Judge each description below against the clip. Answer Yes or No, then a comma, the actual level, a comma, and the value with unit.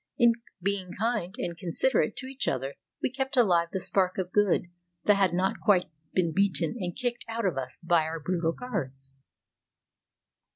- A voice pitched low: No, medium, 185 Hz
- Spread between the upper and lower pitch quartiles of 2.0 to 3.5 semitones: No, average, 4.2 semitones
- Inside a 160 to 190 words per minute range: Yes, average, 170 wpm